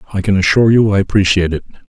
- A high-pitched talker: No, very low, 95 Hz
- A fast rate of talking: Yes, fast, 220 wpm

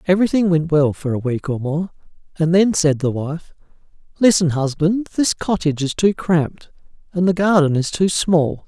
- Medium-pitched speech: Yes, medium, 165 Hz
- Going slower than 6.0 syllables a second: Yes, 5.0 syllables/s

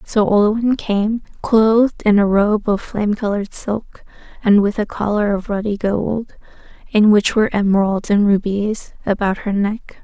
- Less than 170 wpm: Yes, average, 160 wpm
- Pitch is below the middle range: No, high, 210 Hz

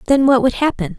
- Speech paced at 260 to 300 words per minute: No, fast, 245 wpm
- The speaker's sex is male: No, female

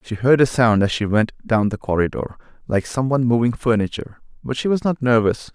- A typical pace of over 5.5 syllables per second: Yes, 5.7 syllables/s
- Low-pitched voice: Yes, low, 120 Hz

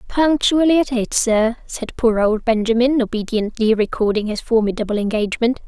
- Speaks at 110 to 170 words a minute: Yes, slow, 135 wpm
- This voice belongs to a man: No, female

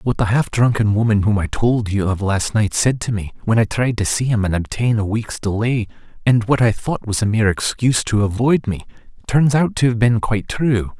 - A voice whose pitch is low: Yes, low, 110 Hz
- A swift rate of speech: Yes, fast, 240 wpm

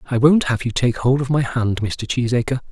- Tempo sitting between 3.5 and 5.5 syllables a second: Yes, 5.4 syllables/s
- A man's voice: Yes, male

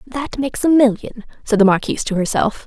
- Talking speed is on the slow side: No, average, 200 wpm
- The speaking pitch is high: Yes, high, 240 Hz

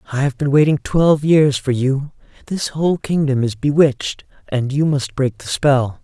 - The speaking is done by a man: Yes, male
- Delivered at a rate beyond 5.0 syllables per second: No, 4.8 syllables/s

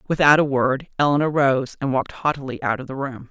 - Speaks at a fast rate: Yes, fast, 220 wpm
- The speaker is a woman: Yes, female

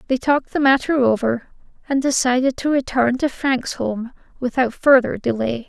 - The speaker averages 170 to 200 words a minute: No, average, 160 wpm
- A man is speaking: No, female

